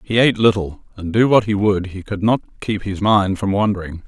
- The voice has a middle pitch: No, low, 100 Hz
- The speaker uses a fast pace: Yes, fast, 235 wpm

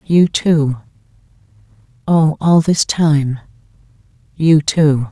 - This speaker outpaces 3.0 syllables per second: No, 2.9 syllables/s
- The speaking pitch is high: No, medium, 140 Hz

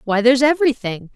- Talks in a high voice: Yes, high, 245 Hz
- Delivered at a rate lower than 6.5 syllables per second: No, 6.9 syllables/s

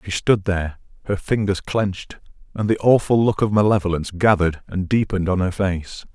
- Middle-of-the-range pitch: No, low, 100 Hz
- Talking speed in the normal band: Yes, average, 175 wpm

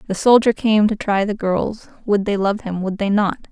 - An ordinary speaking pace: No, fast, 240 wpm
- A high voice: Yes, high, 205 Hz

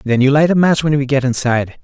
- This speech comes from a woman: No, male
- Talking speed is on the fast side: Yes, fast, 295 wpm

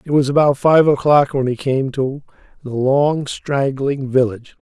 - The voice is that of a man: Yes, male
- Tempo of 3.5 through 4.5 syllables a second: Yes, 4.4 syllables/s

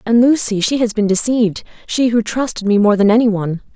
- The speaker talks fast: Yes, fast, 210 wpm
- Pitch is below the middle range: No, high, 220 Hz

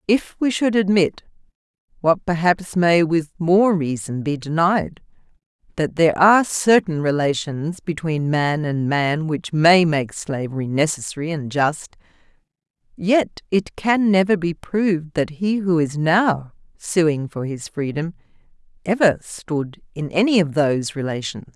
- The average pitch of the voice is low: No, medium, 165 Hz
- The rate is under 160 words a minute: Yes, average, 140 wpm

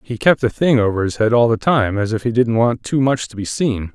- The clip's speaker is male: Yes, male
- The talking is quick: Yes, fast, 305 wpm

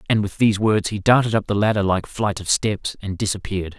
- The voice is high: No, low, 100 Hz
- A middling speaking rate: No, fast, 240 wpm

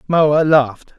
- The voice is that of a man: Yes, male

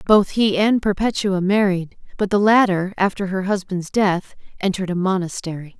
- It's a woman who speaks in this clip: Yes, female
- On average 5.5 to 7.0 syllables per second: No, 5.0 syllables/s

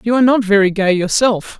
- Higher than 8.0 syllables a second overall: No, 6.0 syllables/s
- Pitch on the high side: Yes, high, 210 Hz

